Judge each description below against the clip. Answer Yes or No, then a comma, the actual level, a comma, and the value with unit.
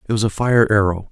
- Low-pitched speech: Yes, low, 105 Hz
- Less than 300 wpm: Yes, fast, 270 wpm